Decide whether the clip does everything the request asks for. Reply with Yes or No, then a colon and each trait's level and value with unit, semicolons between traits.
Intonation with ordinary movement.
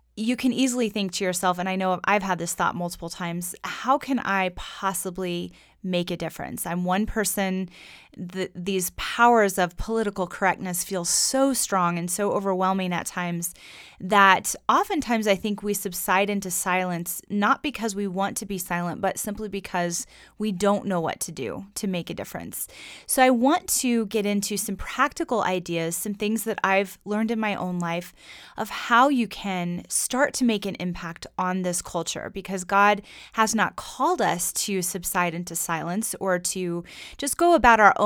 Yes: average, 3.2 semitones